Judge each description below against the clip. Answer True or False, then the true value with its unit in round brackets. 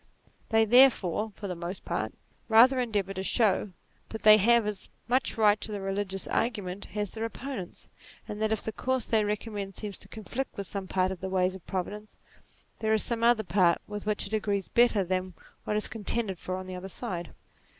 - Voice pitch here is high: True (210 Hz)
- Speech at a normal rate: False (210 wpm)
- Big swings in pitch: False (2.8 semitones)